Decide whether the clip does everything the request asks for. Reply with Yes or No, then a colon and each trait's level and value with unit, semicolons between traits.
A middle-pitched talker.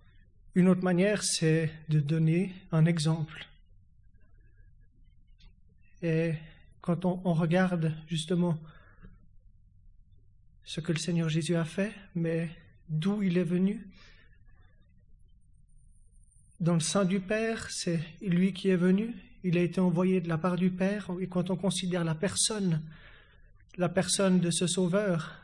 Yes: medium, 165 Hz